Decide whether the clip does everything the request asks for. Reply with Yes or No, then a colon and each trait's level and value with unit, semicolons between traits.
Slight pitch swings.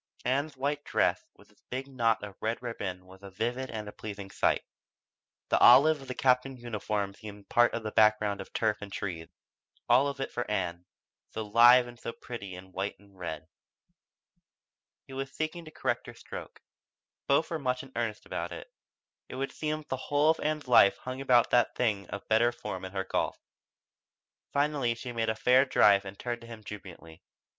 No: average, 4.5 semitones